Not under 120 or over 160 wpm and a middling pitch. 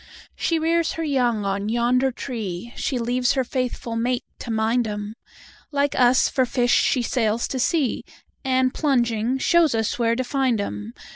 No: average, 150 wpm; high, 245 Hz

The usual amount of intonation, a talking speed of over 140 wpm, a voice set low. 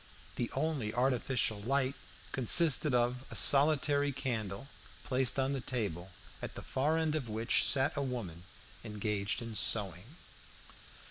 No: average, 4.3 semitones; slow, 135 wpm; low, 125 Hz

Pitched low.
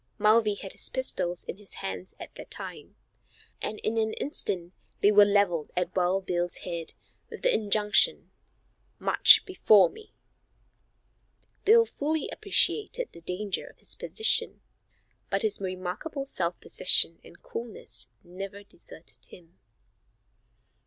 No: high, 200 Hz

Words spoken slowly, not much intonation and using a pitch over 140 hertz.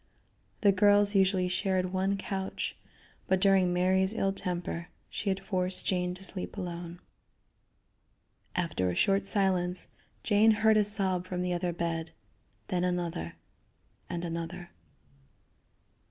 Yes: slow, 125 wpm; narrow, 1.7 semitones; medium, 185 Hz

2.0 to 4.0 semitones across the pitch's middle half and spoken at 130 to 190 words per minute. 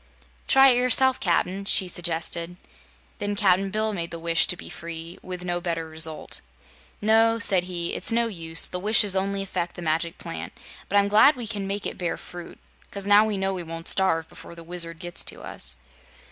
No: average, 3.4 semitones; average, 200 wpm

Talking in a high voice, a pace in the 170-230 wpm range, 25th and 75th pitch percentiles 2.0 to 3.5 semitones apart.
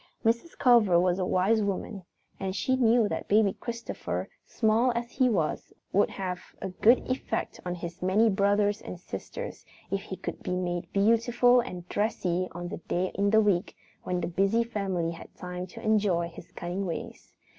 No: high, 200 Hz; average, 180 wpm; average, 3.9 semitones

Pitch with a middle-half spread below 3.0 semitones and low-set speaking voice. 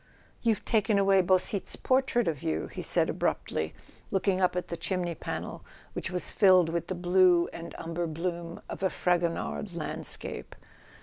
No: narrow, 2.4 semitones; medium, 180 Hz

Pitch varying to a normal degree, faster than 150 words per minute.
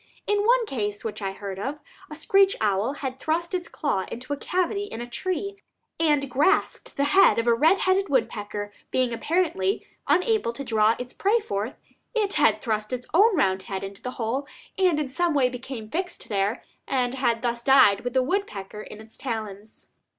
No: wide, 8.0 semitones; average, 190 wpm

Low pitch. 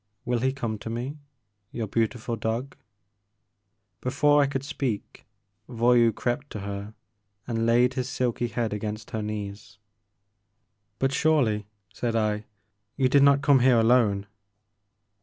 Yes: low, 115 Hz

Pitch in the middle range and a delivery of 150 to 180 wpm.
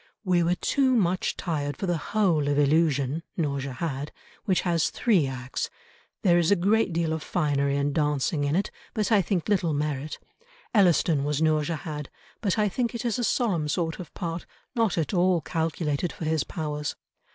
Yes: medium, 165 Hz; average, 175 wpm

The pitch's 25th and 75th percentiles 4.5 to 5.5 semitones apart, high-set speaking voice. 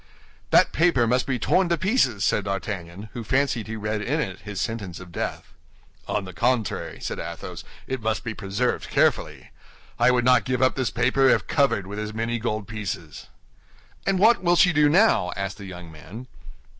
No: average, 5.0 semitones; low, 115 Hz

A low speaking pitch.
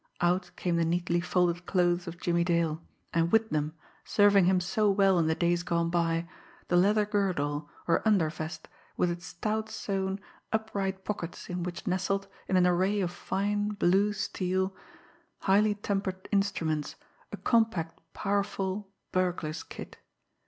No: medium, 180 Hz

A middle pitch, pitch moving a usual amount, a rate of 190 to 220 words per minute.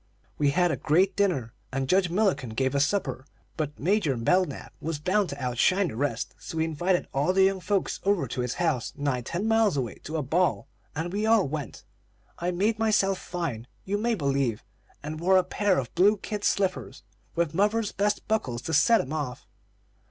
No: medium, 170 Hz; wide, 6.1 semitones; average, 195 wpm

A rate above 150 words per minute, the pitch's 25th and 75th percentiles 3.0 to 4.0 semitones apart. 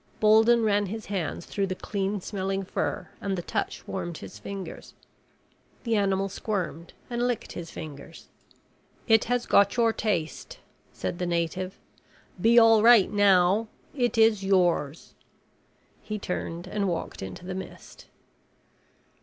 No: slow, 135 wpm; average, 3.5 semitones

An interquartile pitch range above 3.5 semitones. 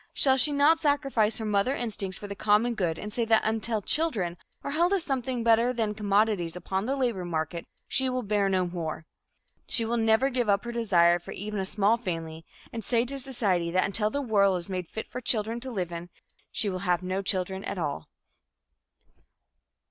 Yes: average, 4.6 semitones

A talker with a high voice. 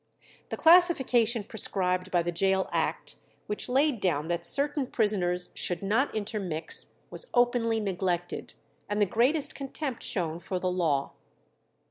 Yes: high, 205 Hz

